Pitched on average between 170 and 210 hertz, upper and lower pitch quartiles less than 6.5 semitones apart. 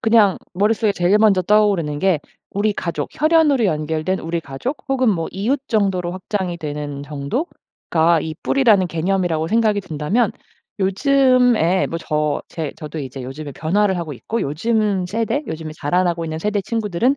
Yes: medium, 185 Hz; wide, 5.4 semitones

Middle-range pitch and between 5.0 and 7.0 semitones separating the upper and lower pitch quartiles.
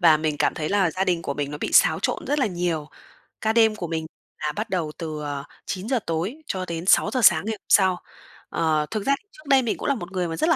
Yes: medium, 180 Hz; average, 5.3 semitones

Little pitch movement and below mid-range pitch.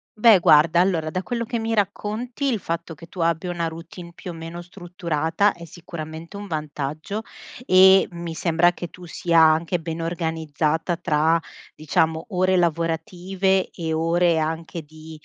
No: narrow, 2.3 semitones; medium, 170 Hz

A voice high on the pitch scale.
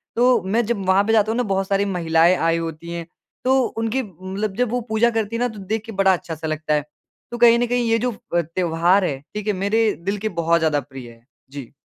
Yes: high, 195 Hz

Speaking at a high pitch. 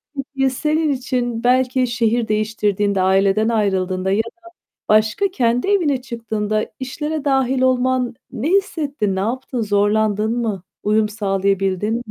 Yes: high, 230 Hz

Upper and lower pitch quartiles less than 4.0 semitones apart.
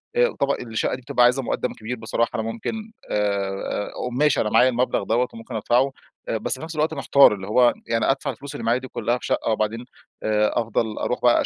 Yes: average, 3.0 semitones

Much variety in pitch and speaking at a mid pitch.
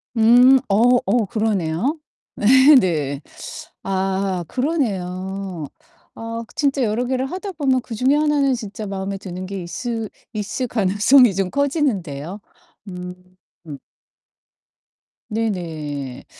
No: wide, 5.7 semitones; high, 210 Hz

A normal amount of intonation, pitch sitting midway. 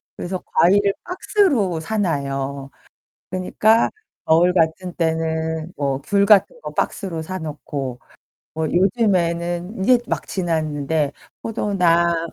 Yes: average, 3.7 semitones; medium, 170 Hz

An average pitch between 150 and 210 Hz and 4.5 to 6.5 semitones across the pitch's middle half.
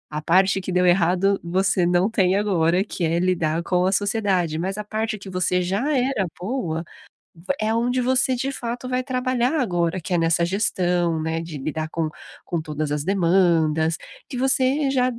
Yes: medium, 185 Hz; average, 5.1 semitones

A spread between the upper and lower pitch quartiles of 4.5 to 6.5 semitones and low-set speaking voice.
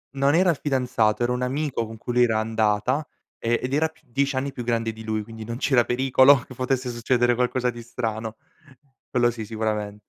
No: average, 2.7 semitones; low, 120 Hz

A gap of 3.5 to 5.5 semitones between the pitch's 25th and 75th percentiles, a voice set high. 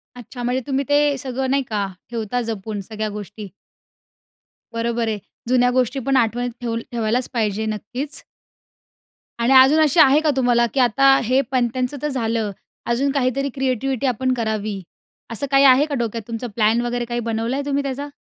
No: average, 3.1 semitones; high, 245 Hz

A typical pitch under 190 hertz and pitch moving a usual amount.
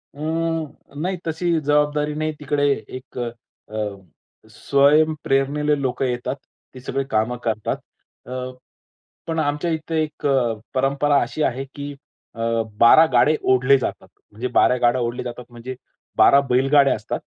Yes: medium, 140 Hz; average, 3.3 semitones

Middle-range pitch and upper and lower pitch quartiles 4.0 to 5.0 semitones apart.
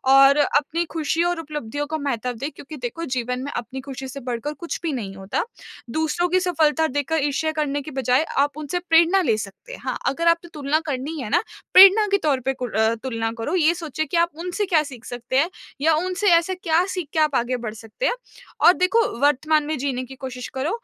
No: very high, 295 Hz; average, 4.4 semitones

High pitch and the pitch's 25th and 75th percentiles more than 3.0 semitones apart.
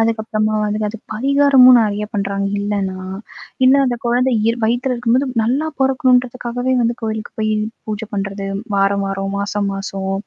Yes: high, 220 Hz; average, 3.7 semitones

